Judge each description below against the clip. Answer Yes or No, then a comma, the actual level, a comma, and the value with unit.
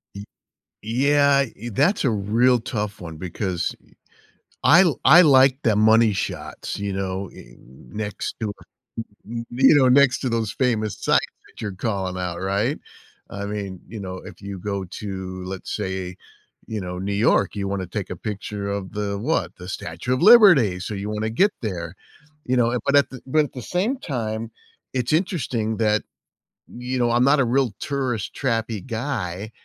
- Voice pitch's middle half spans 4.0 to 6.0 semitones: Yes, average, 4.7 semitones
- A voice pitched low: Yes, low, 110 Hz